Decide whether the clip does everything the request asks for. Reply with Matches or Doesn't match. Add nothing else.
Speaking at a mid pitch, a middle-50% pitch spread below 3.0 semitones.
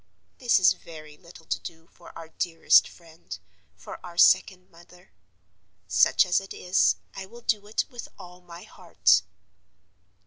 Matches